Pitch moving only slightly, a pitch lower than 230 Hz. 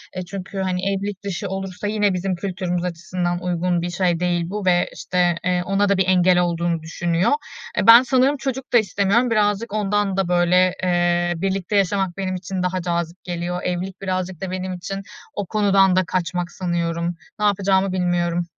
Yes: narrow, 1.9 semitones; medium, 185 Hz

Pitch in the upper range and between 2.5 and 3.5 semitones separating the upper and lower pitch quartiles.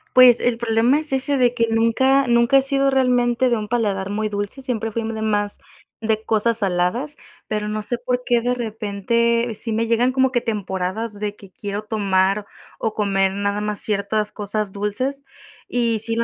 Yes: high, 225 Hz; average, 2.9 semitones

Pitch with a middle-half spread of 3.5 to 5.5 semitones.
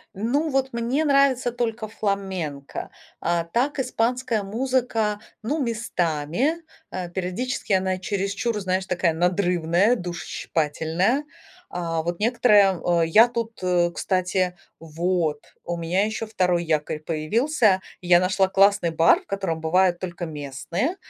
Yes: average, 5.1 semitones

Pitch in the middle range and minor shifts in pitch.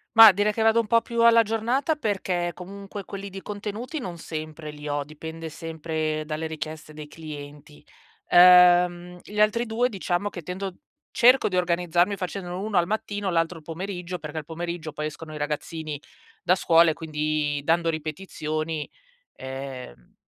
No: medium, 175 Hz; average, 4.4 semitones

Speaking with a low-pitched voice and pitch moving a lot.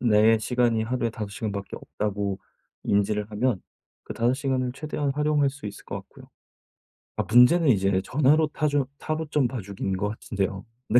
No: low, 120 Hz; average, 5.0 semitones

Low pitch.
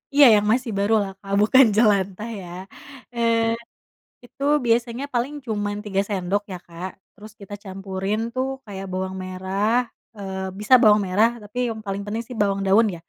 No: high, 205 Hz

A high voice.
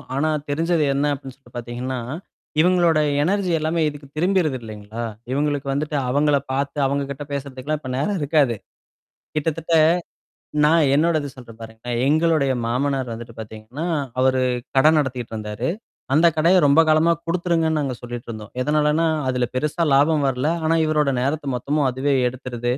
No: medium, 140 Hz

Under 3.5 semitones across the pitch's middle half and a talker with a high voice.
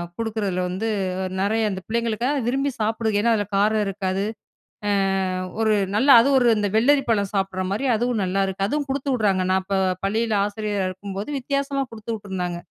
Yes: average, 3.1 semitones; high, 215 Hz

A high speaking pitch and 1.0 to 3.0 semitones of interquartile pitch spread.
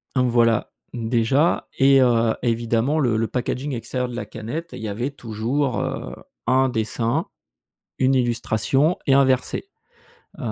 No: low, 125 Hz; average, 2.7 semitones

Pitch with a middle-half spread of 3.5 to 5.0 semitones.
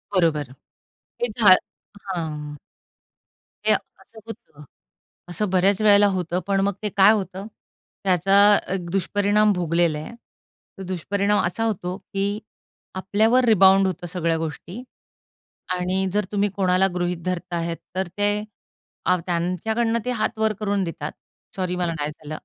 No: average, 2.9 semitones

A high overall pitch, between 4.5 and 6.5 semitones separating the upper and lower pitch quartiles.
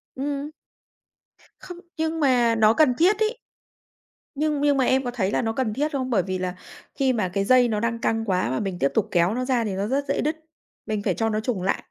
Yes: high, 240 Hz; average, 5.1 semitones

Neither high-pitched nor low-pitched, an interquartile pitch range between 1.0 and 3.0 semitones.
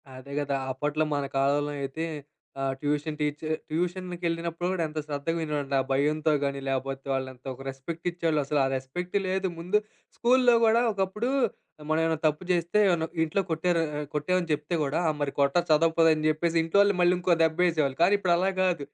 No: medium, 160 Hz; average, 3.6 semitones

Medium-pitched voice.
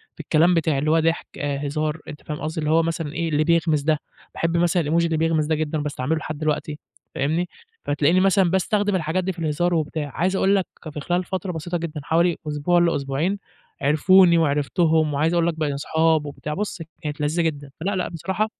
Yes: medium, 160 Hz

